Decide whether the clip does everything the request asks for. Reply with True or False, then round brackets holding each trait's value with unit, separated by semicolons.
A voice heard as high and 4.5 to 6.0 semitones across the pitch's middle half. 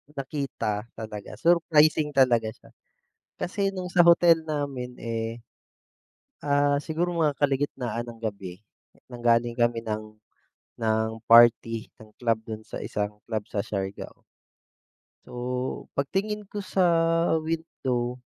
False (125 Hz; 5.5 semitones)